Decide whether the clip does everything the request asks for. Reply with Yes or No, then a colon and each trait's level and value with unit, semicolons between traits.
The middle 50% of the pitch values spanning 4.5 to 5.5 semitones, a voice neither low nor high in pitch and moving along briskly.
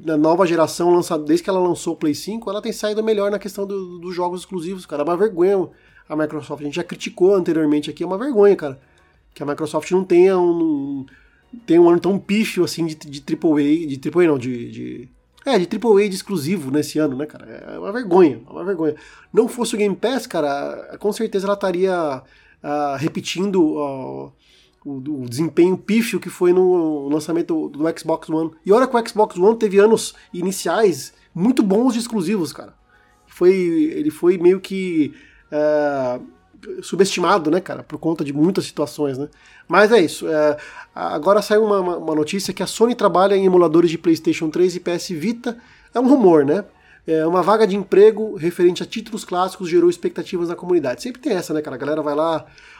Yes: average, 4.8 semitones; medium, 180 Hz; fast, 195 wpm